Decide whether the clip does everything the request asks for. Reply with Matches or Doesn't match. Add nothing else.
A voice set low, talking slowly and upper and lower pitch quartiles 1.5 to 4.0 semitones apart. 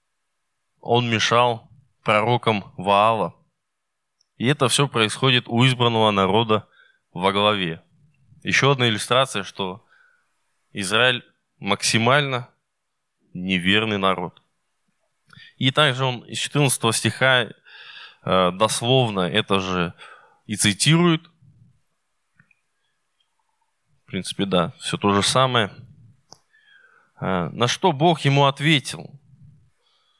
Doesn't match